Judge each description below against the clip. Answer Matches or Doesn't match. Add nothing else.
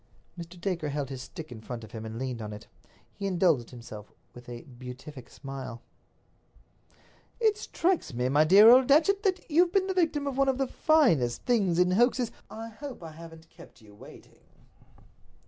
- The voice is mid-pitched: Matches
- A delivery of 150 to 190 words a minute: Matches